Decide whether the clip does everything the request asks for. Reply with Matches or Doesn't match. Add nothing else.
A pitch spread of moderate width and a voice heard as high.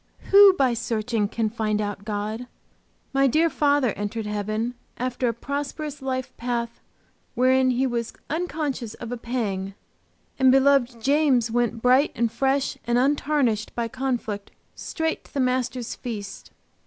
Matches